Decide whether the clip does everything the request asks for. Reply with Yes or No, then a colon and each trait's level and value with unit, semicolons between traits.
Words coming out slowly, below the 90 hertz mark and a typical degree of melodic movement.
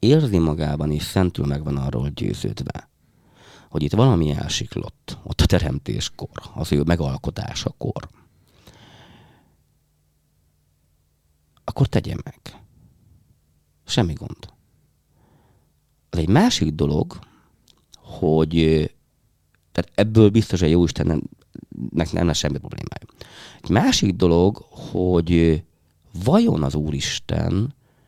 Yes: slow, 95 wpm; very low, 80 Hz; average, 3.1 semitones